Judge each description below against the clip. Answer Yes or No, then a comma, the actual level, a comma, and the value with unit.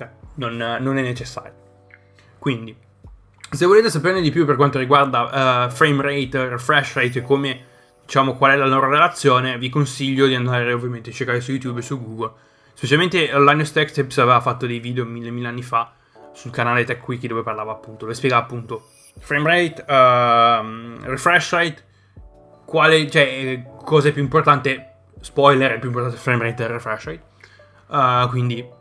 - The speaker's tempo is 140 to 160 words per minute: No, fast, 170 wpm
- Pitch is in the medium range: No, low, 125 Hz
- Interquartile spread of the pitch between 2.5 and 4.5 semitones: Yes, average, 3.3 semitones